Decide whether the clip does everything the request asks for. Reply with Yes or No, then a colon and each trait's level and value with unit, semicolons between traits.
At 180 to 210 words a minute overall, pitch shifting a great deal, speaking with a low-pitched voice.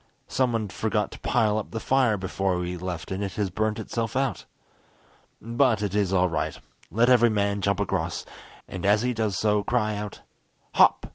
No: average, 185 wpm; average, 2.9 semitones; low, 105 Hz